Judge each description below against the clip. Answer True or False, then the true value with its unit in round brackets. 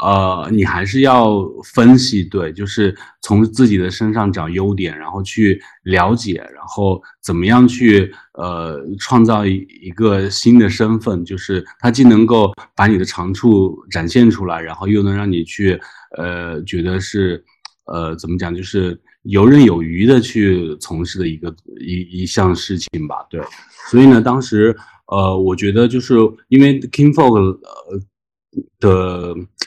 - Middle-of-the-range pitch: False (100 Hz)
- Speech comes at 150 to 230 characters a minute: True (225 characters per minute)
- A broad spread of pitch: False (3.7 semitones)